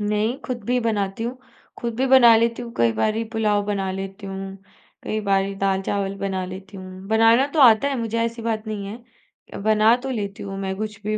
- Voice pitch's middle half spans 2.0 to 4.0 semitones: Yes, average, 2.9 semitones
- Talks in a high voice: Yes, high, 215 Hz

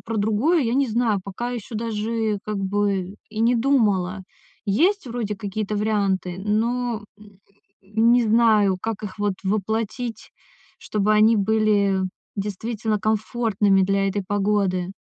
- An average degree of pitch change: No, narrow, 2.3 semitones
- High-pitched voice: Yes, high, 210 Hz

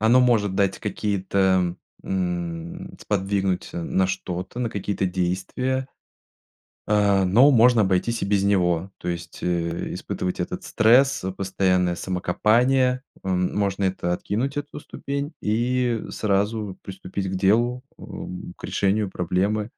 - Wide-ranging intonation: No, average, 3.8 semitones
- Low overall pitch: Yes, low, 100 Hz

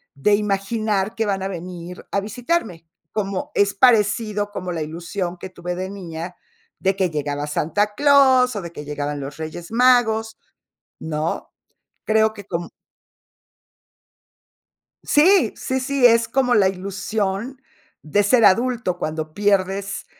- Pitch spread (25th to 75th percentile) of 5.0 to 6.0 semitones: No, average, 4.3 semitones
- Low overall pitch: No, high, 200 Hz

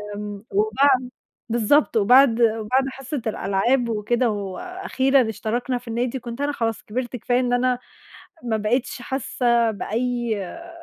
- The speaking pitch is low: No, high, 240 Hz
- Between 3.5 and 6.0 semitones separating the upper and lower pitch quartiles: No, average, 2.8 semitones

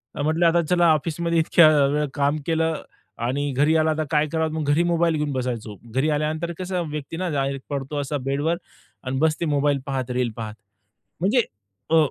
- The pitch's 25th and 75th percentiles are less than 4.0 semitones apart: Yes, average, 2.9 semitones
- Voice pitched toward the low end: No, medium, 150 Hz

